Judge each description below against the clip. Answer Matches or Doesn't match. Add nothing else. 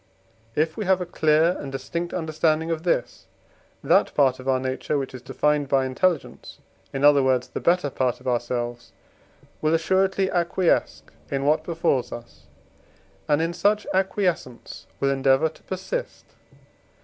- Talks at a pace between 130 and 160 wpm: Matches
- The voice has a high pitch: Doesn't match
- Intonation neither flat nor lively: Matches